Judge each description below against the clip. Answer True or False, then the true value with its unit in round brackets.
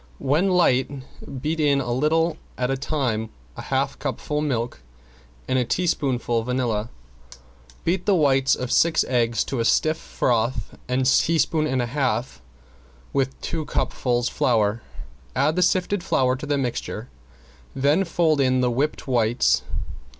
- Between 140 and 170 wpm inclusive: True (150 wpm)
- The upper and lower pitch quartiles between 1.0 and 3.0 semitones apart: False (4.1 semitones)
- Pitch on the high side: False (130 Hz)